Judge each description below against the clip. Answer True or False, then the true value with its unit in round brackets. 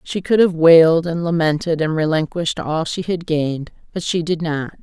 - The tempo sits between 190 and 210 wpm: True (200 wpm)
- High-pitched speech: False (165 Hz)